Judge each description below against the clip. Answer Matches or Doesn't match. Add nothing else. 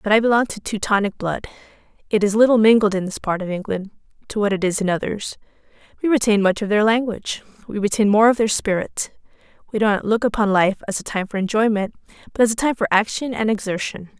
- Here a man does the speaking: Doesn't match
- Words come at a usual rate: Doesn't match